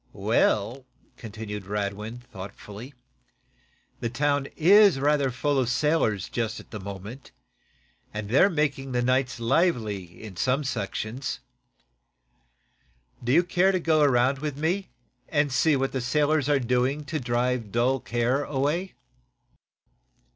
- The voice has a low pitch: Yes, low, 130 Hz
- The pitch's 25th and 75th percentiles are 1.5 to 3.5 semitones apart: No, average, 4.3 semitones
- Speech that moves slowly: Yes, slow, 125 wpm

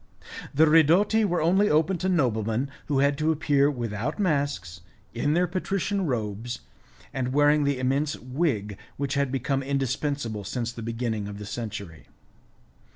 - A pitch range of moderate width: Yes, average, 5.0 semitones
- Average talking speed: Yes, average, 150 wpm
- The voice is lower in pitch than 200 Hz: Yes, medium, 140 Hz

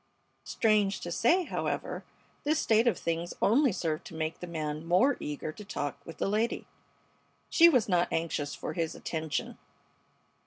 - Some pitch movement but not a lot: No, wide, 5.9 semitones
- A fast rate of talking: No, average, 160 wpm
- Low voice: No, medium, 175 Hz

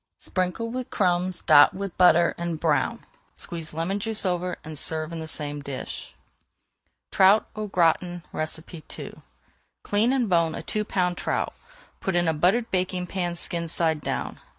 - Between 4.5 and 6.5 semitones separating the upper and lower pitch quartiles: No, average, 2.9 semitones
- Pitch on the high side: No, medium, 175 Hz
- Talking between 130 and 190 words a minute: Yes, average, 155 wpm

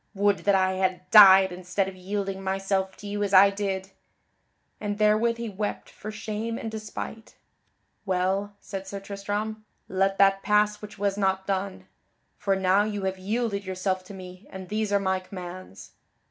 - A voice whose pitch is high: Yes, high, 195 Hz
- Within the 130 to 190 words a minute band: Yes, average, 170 wpm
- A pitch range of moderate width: No, narrow, 1.6 semitones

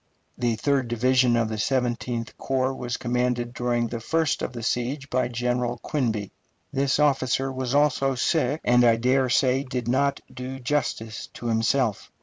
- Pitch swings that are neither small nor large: No, narrow, 2.0 semitones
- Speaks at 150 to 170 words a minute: Yes, average, 160 wpm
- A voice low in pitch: Yes, low, 125 Hz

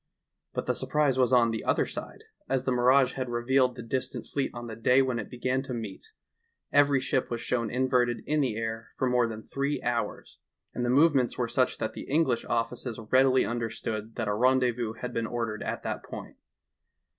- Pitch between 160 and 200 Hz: No, low, 125 Hz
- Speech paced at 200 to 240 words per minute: Yes, fast, 205 wpm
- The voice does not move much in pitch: Yes, narrow, 2.2 semitones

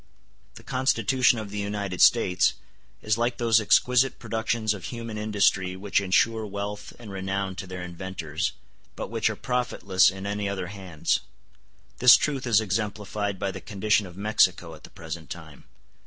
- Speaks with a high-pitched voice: No, low, 100 Hz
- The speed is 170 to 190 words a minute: No, average, 160 wpm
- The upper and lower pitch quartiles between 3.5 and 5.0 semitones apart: No, average, 3.0 semitones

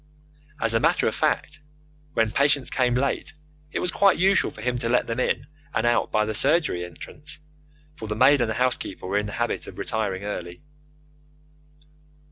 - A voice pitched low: Yes, low, 120 Hz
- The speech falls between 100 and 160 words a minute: No, average, 185 wpm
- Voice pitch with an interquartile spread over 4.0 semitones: Yes, average, 4.8 semitones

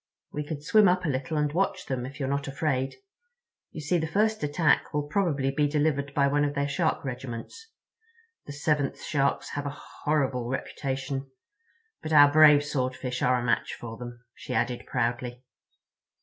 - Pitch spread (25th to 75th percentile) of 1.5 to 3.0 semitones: Yes, narrow, 2.5 semitones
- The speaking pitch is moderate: Yes, medium, 145 Hz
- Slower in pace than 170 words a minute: No, average, 175 wpm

